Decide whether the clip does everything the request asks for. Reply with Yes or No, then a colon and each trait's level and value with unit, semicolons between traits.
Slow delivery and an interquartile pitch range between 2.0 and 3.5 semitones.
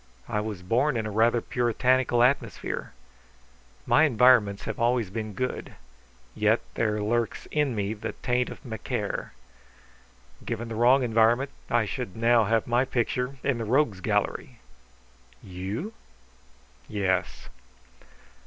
Yes: slow, 125 wpm; average, 2.8 semitones